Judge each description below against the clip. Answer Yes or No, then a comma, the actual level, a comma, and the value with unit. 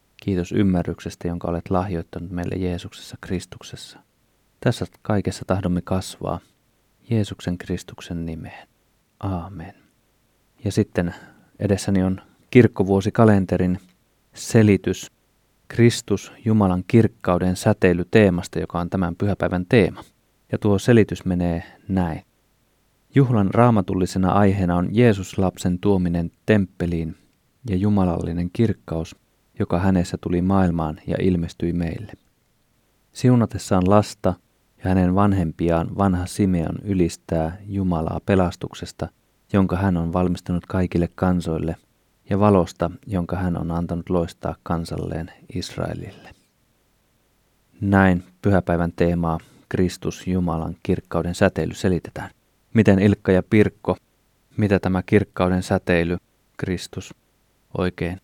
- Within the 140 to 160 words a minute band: No, average, 100 wpm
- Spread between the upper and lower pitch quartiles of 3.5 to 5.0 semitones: No, average, 2.7 semitones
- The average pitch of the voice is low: Yes, very low, 95 Hz